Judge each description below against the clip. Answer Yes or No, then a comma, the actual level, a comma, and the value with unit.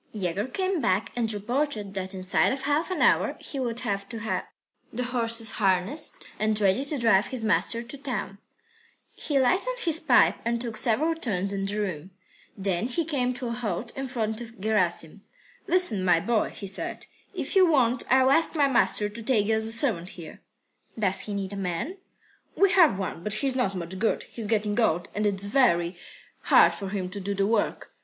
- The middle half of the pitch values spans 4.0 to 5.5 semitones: Yes, average, 4.7 semitones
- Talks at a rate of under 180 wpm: No, average, 200 wpm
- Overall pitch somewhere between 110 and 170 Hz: No, high, 220 Hz